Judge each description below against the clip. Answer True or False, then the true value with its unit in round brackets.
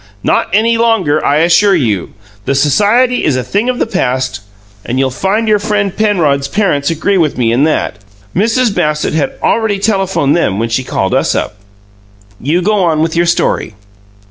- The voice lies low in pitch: False (170 Hz)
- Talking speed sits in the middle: True (180 wpm)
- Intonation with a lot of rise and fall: True (6.9 semitones)